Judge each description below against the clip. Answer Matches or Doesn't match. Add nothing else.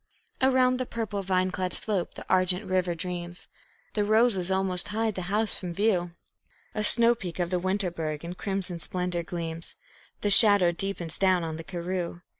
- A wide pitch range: Doesn't match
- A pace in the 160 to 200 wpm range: Matches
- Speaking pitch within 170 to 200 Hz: Matches